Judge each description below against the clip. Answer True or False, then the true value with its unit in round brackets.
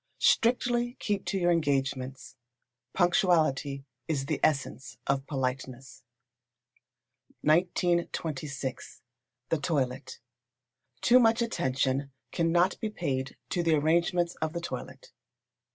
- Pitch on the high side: False (155 Hz)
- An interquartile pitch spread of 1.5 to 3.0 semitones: False (4.6 semitones)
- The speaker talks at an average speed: False (100 wpm)